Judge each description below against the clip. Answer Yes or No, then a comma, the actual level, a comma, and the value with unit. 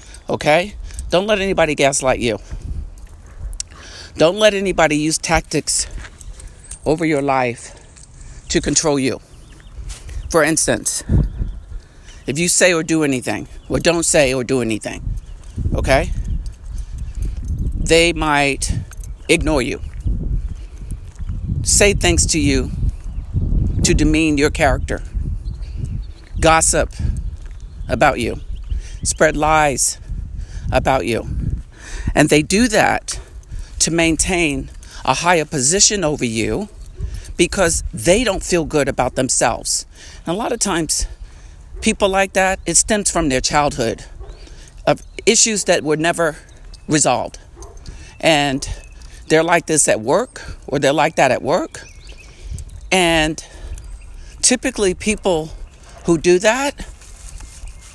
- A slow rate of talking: Yes, slow, 110 wpm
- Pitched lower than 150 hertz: Yes, low, 135 Hz